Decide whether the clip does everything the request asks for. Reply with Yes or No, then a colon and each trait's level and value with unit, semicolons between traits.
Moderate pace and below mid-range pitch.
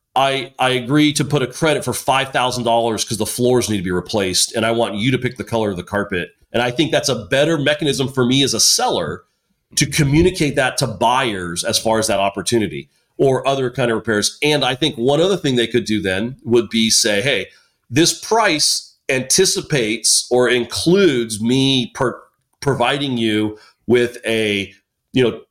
Yes: average, 190 wpm; low, 120 Hz